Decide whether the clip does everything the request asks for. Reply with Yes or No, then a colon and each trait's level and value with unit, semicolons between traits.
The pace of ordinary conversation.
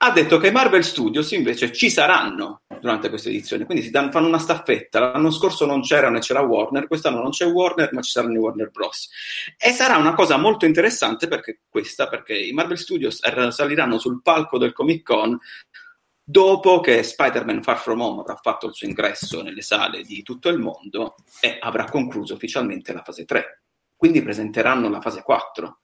No: fast, 190 wpm